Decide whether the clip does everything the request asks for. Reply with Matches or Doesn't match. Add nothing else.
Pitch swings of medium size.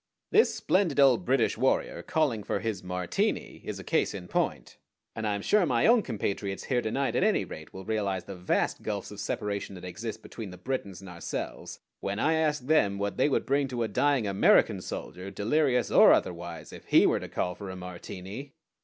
Doesn't match